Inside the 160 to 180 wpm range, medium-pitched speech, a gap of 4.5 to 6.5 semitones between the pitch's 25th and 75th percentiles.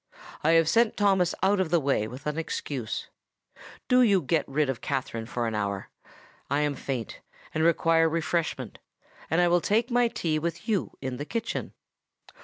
Yes: average, 175 wpm; medium, 160 Hz; average, 5.1 semitones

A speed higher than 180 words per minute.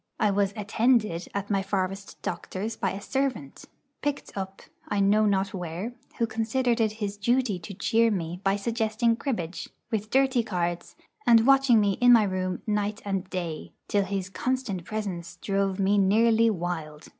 No: average, 165 wpm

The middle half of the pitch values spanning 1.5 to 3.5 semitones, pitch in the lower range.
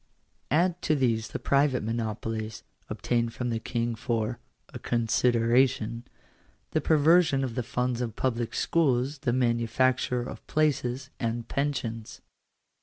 Yes: narrow, 2.6 semitones; low, 120 Hz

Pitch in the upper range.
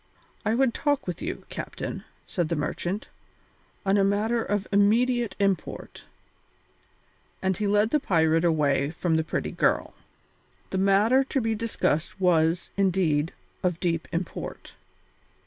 Yes: high, 195 Hz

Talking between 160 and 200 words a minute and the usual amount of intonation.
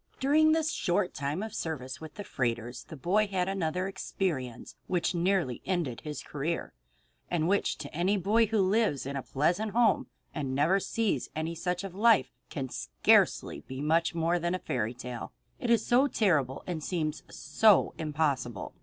No: average, 170 wpm; wide, 5.8 semitones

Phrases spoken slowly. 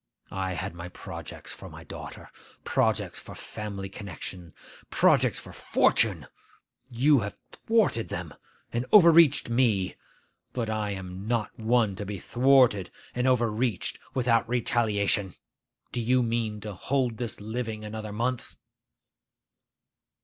Yes: slow, 125 wpm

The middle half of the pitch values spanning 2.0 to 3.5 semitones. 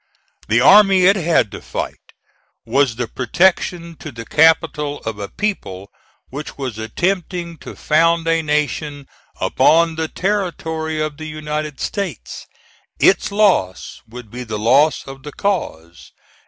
No: average, 5.2 semitones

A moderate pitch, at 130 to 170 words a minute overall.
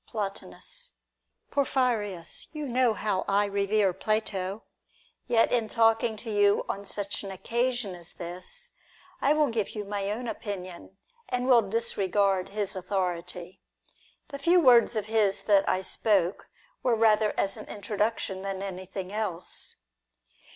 No: high, 205 Hz; slow, 135 wpm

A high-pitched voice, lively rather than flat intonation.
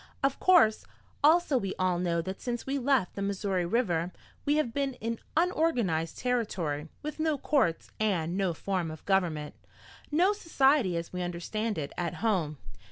Yes: high, 200 Hz; wide, 7.8 semitones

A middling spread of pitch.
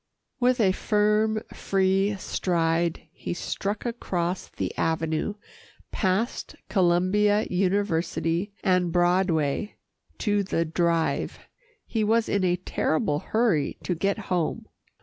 Yes: average, 3.5 semitones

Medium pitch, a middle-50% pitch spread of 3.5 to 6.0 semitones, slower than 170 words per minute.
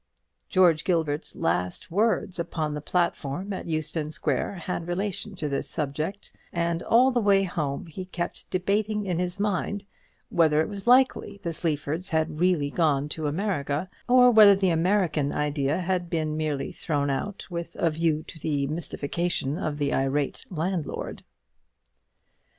Yes: medium, 170 Hz; average, 3.9 semitones; average, 150 wpm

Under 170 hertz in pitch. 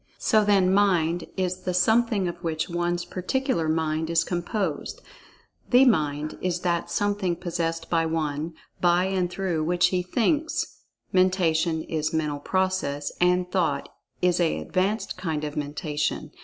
No: medium, 175 Hz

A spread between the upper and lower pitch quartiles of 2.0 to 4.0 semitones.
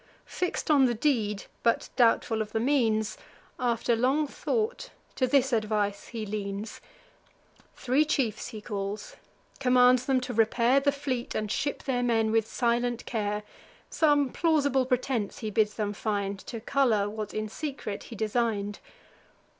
Yes: average, 3.7 semitones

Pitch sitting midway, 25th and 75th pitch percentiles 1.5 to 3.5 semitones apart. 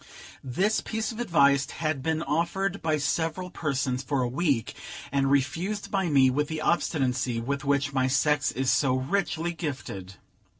No: medium, 145 Hz; average, 4.2 semitones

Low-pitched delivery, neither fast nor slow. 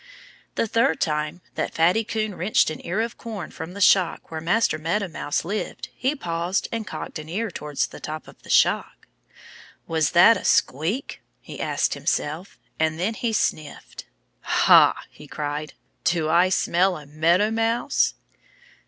No: medium, 175 Hz; average, 160 wpm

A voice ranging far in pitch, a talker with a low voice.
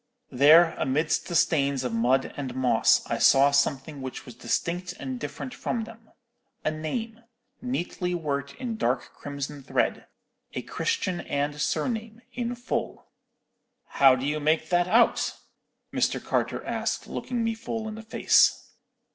No: wide, 8.0 semitones; medium, 155 Hz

